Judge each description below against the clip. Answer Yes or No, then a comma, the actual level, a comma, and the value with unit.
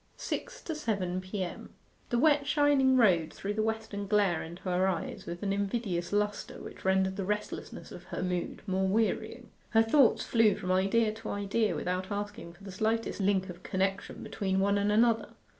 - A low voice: No, high, 200 Hz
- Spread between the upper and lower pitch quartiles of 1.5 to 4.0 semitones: Yes, average, 2.8 semitones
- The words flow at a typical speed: Yes, average, 180 wpm